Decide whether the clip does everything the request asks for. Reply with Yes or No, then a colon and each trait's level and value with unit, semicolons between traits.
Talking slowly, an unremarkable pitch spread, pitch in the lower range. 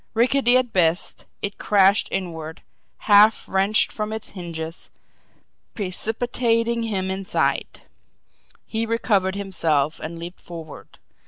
No: slow, 105 wpm; average, 4.5 semitones; high, 195 Hz